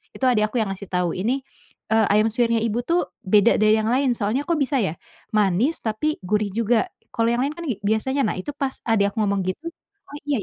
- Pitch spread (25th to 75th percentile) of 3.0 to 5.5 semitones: Yes, average, 4.1 semitones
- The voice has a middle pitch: No, high, 225 Hz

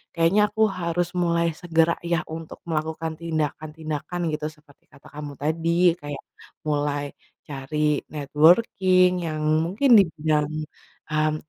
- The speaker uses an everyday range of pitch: No, narrow, 2.0 semitones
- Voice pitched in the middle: Yes, medium, 160 Hz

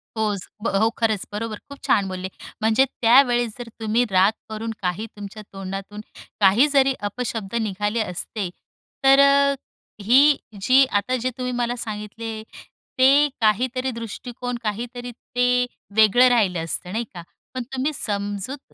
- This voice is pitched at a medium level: No, high, 225 Hz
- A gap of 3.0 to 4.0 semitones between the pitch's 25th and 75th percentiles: Yes, average, 3.5 semitones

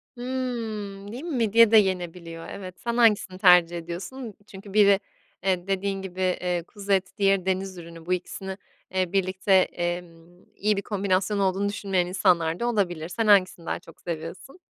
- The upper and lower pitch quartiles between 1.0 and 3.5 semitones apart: Yes, narrow, 2.4 semitones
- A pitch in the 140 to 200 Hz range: Yes, high, 190 Hz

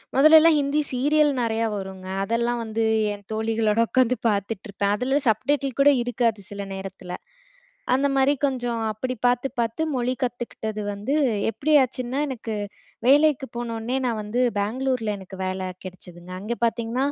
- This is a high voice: Yes, high, 235 Hz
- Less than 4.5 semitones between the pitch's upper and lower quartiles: Yes, average, 3.9 semitones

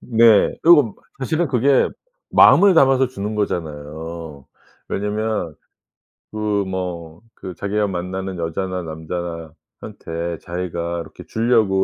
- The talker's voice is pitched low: Yes, very low, 95 Hz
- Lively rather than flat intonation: No, average, 4.7 semitones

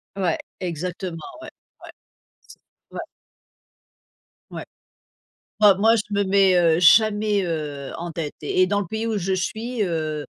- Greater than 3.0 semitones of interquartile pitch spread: Yes, average, 3.9 semitones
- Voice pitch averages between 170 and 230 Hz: Yes, medium, 185 Hz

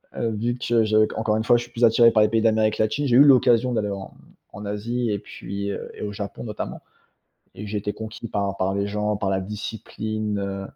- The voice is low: Yes, low, 110 Hz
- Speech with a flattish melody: Yes, narrow, 2.2 semitones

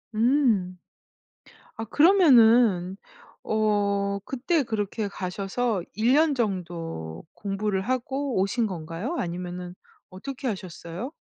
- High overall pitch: Yes, high, 205 Hz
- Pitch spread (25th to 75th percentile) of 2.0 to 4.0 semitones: No, average, 5.2 semitones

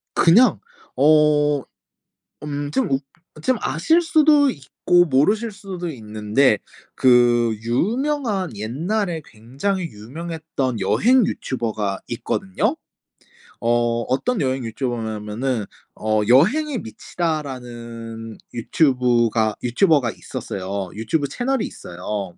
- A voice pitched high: No, low, 135 Hz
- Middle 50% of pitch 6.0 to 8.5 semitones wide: Yes, wide, 7.6 semitones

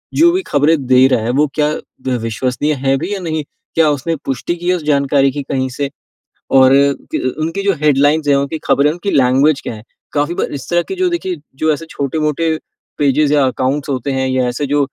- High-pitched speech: No, medium, 145 Hz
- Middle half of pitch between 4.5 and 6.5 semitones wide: No, average, 3.0 semitones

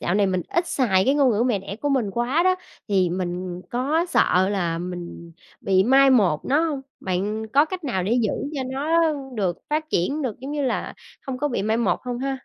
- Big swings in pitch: Yes, wide, 6.6 semitones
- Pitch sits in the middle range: No, high, 235 Hz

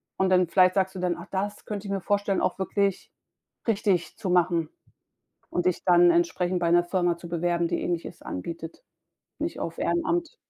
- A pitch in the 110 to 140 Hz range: No, medium, 180 Hz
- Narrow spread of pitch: Yes, narrow, 2.3 semitones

